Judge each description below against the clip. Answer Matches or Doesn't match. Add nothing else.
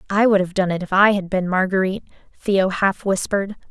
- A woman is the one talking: Matches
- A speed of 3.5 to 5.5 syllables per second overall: Doesn't match